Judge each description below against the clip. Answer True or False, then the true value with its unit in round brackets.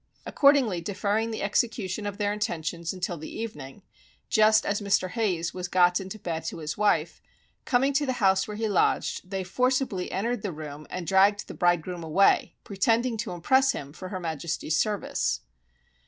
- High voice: True (195 Hz)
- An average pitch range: True (4.0 semitones)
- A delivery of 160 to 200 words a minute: True (170 wpm)